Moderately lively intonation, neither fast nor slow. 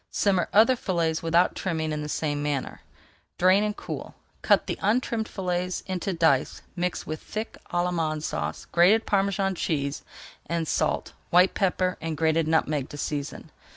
Yes: average, 3.5 semitones; average, 155 wpm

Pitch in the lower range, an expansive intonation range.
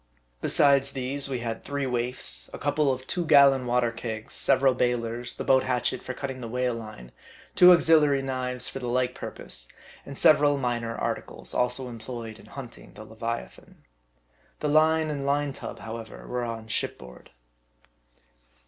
No: low, 125 Hz; average, 3.1 semitones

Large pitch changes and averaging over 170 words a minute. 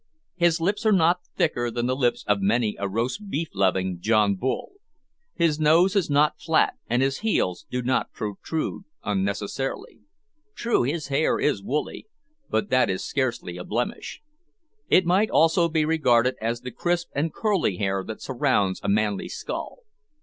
No: wide, 7.6 semitones; average, 165 wpm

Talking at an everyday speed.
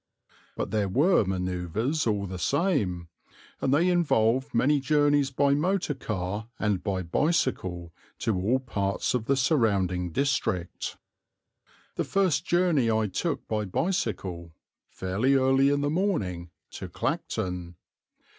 No: slow, 125 wpm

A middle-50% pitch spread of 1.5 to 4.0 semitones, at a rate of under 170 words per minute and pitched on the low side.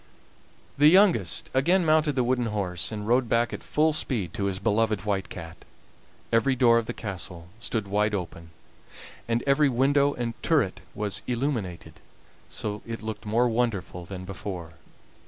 No: average, 4.8 semitones; average, 155 wpm; low, 115 Hz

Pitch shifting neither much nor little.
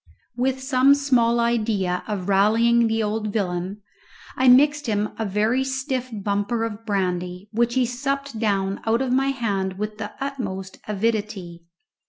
Yes: average, 4.0 semitones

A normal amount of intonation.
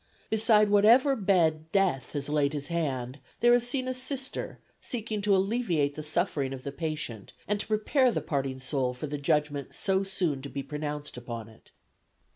No: wide, 7.0 semitones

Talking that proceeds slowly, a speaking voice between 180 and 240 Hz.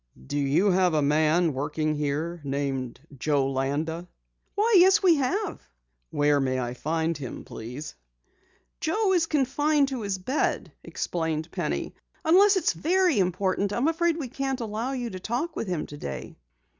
No: average, 160 wpm; medium, 185 Hz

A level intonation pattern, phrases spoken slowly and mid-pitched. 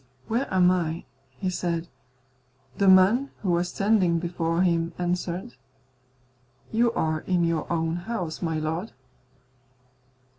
Yes: narrow, 2.1 semitones; slow, 120 wpm; medium, 175 Hz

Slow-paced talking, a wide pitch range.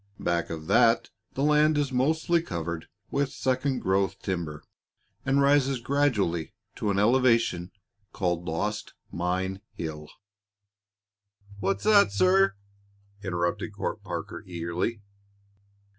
Yes: slow, 115 wpm; wide, 6.7 semitones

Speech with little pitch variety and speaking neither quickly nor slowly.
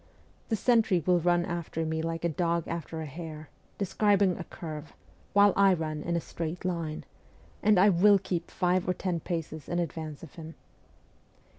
Yes: narrow, 2.3 semitones; average, 175 wpm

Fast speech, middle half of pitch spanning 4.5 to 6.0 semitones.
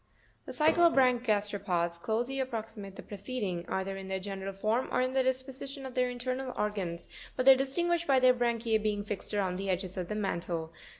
Yes: fast, 215 wpm; average, 4.9 semitones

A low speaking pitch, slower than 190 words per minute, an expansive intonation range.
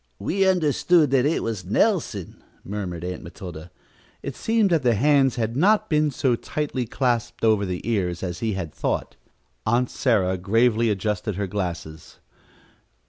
Yes: low, 115 Hz; average, 150 wpm; wide, 6.6 semitones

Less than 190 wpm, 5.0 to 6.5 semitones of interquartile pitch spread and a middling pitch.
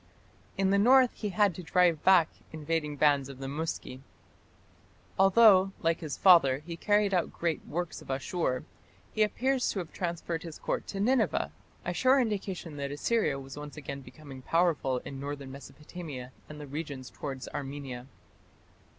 Yes: average, 160 wpm; wide, 5.4 semitones; medium, 160 Hz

